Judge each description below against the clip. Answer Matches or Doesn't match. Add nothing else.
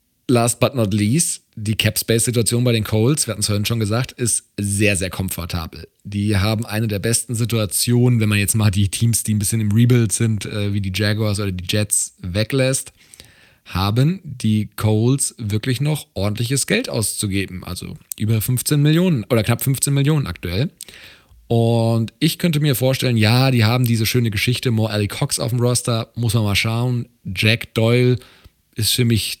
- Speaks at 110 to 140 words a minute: Doesn't match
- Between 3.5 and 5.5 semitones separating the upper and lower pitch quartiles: Doesn't match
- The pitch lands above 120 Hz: Doesn't match